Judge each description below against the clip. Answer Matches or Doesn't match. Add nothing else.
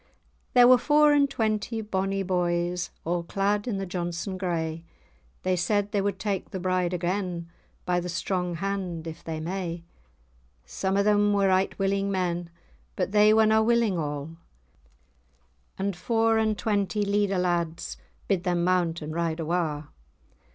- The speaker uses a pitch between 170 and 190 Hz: Matches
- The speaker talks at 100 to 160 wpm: Matches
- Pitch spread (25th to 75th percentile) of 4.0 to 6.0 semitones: Doesn't match